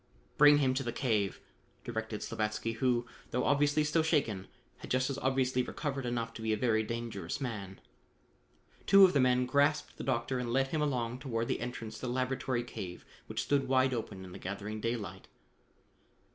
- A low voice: Yes, low, 125 Hz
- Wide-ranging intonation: No, average, 3.1 semitones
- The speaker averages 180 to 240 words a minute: Yes, average, 185 wpm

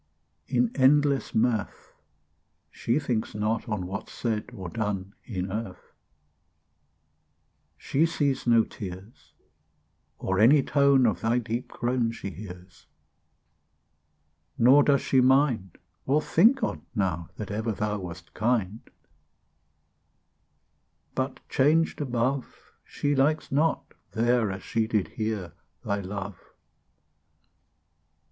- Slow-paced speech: Yes, slow, 110 wpm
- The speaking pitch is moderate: No, low, 115 Hz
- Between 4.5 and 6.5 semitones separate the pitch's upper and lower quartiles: Yes, average, 5.0 semitones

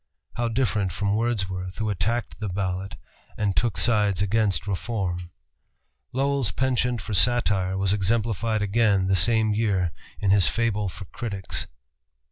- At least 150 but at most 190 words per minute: No, slow, 135 wpm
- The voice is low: Yes, low, 105 Hz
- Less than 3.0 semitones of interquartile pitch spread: No, average, 3.3 semitones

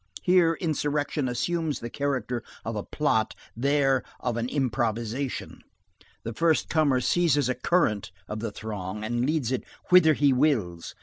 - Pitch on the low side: Yes, low, 130 Hz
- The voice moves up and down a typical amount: Yes, average, 4.7 semitones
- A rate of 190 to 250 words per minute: No, average, 145 wpm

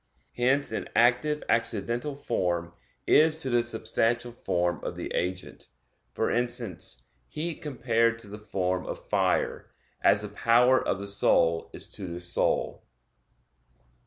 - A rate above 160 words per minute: No, slow, 135 wpm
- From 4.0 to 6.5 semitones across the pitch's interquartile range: Yes, average, 4.4 semitones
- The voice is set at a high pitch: No, low, 115 Hz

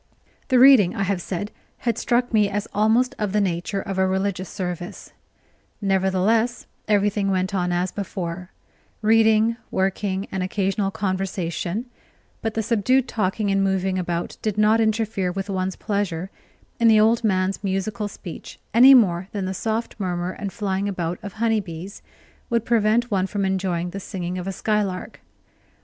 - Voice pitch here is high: Yes, high, 195 Hz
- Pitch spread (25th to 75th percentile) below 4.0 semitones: Yes, average, 2.7 semitones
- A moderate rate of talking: Yes, average, 160 wpm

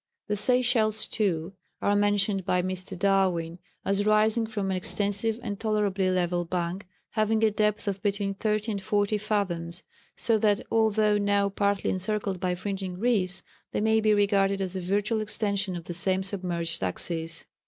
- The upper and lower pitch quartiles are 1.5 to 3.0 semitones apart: Yes, narrow, 2.4 semitones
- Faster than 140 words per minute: Yes, average, 165 wpm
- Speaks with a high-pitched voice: Yes, high, 200 Hz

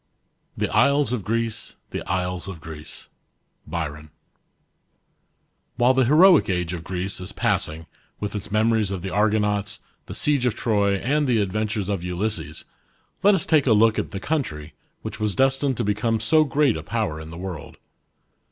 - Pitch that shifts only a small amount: No, average, 5.1 semitones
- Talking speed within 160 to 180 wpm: Yes, average, 170 wpm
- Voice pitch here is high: No, low, 105 Hz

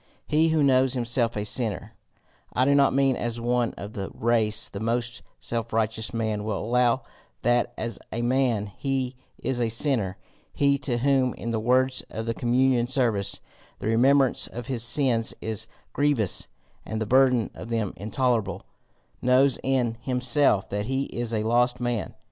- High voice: No, low, 120 Hz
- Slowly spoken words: No, average, 165 wpm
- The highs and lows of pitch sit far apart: No, average, 2.8 semitones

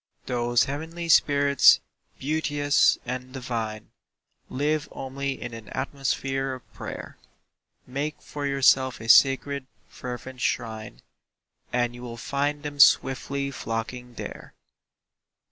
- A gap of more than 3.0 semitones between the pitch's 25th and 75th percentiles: No, narrow, 2.5 semitones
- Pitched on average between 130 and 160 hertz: Yes, low, 135 Hz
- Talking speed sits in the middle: No, slow, 110 wpm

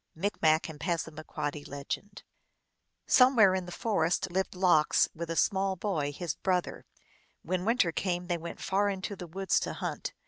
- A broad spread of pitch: No, average, 3.0 semitones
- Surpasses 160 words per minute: No, average, 150 wpm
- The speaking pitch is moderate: Yes, medium, 180 Hz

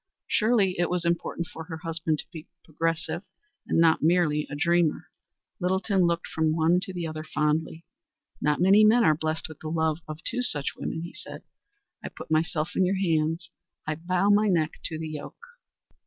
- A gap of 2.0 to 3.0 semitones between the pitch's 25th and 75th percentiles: Yes, narrow, 2.4 semitones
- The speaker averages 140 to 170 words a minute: No, average, 185 wpm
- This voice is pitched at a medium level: Yes, medium, 165 Hz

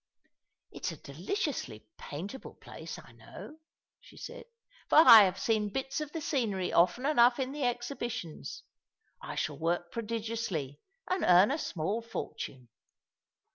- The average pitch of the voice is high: Yes, high, 230 Hz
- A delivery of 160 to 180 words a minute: No, average, 140 wpm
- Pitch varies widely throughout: Yes, wide, 7.4 semitones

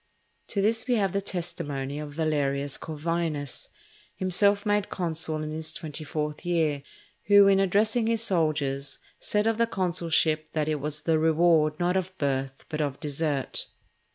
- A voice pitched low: No, medium, 160 Hz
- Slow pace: No, average, 155 wpm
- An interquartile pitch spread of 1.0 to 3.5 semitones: No, average, 4.2 semitones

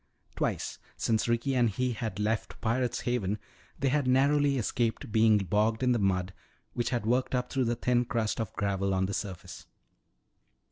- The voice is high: No, low, 115 Hz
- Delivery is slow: No, average, 175 wpm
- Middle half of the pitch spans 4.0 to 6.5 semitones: No, average, 3.2 semitones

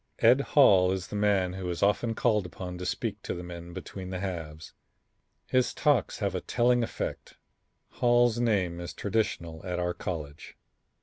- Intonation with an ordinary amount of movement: Yes, average, 3.8 semitones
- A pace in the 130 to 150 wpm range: No, average, 170 wpm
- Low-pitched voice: Yes, very low, 95 Hz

